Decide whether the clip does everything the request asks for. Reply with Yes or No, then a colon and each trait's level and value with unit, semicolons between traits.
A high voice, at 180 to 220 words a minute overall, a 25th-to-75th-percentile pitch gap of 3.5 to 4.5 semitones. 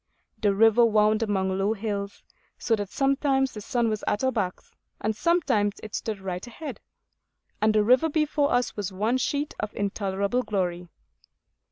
No: high, 215 Hz; average, 165 wpm; average, 3.8 semitones